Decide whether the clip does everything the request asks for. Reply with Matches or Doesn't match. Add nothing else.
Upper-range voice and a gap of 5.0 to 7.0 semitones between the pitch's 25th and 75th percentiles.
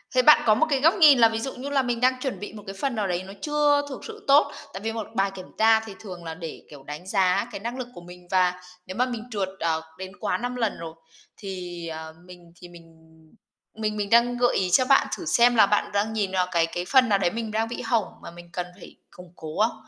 Matches